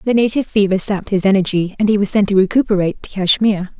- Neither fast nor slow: No, fast, 220 wpm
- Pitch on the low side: No, high, 200 Hz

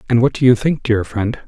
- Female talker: No, male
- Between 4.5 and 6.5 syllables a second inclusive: Yes, 5.7 syllables/s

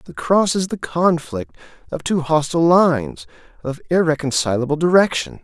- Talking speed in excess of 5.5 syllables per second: No, 5.0 syllables/s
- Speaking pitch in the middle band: Yes, medium, 155 Hz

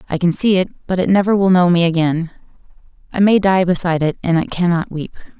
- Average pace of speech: No, fast, 225 wpm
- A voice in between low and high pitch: Yes, medium, 175 Hz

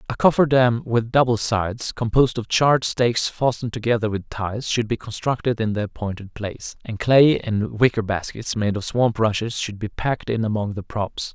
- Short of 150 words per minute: No, average, 190 wpm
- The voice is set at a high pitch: No, low, 115 Hz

